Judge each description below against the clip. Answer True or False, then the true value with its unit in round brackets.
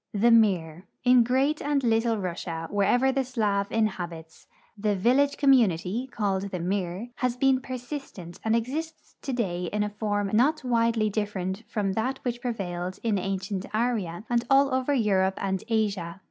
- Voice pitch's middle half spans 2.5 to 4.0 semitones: False (4.6 semitones)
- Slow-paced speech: False (160 wpm)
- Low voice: False (215 Hz)